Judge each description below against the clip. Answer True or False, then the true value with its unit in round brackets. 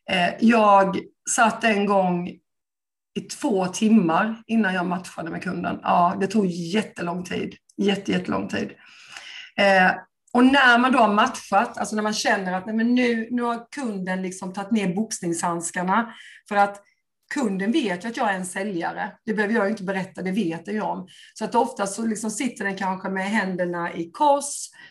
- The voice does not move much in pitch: False (3.3 semitones)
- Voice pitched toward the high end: True (200 Hz)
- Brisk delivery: False (170 wpm)